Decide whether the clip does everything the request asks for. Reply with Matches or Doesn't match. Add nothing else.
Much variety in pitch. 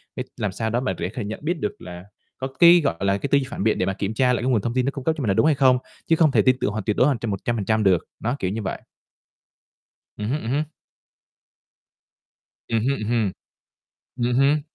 Doesn't match